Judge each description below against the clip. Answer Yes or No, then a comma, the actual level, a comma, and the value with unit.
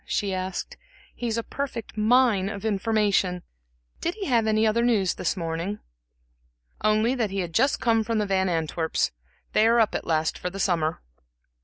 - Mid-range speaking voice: No, high, 210 Hz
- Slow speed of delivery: No, average, 175 wpm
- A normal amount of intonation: Yes, average, 3.7 semitones